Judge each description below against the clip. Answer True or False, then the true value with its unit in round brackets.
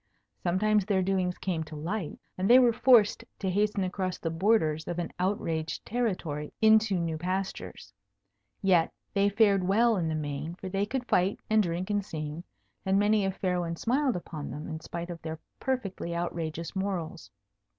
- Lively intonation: False (3.7 semitones)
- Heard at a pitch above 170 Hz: True (185 Hz)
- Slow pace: False (175 wpm)